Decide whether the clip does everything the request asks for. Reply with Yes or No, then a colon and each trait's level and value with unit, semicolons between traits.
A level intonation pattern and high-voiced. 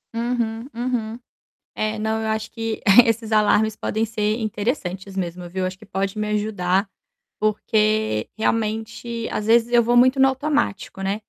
Yes: narrow, 1.9 semitones; high, 220 Hz